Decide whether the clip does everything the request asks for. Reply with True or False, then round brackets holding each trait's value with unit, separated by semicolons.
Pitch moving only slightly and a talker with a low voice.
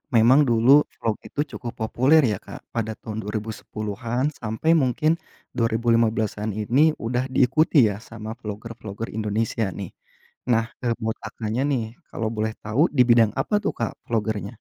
True (1.8 semitones; 115 Hz)